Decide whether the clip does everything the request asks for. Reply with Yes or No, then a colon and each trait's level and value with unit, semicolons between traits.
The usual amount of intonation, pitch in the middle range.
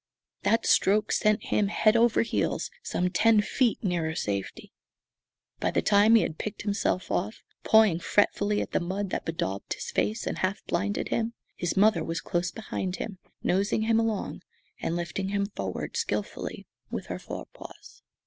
No: average, 3.4 semitones; high, 200 Hz